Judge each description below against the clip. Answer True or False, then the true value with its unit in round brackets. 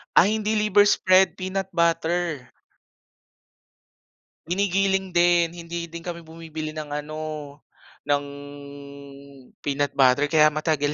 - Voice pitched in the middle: True (170 Hz)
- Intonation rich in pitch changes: False (3.3 semitones)